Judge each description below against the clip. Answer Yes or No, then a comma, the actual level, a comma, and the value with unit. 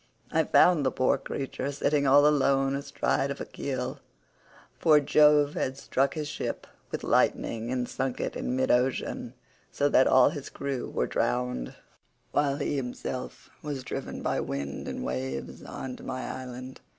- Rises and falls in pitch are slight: Yes, narrow, 2.1 semitones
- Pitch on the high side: No, low, 135 Hz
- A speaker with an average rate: Yes, average, 160 wpm